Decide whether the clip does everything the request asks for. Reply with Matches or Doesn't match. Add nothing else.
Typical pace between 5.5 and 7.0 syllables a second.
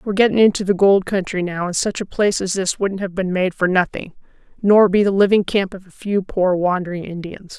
Matches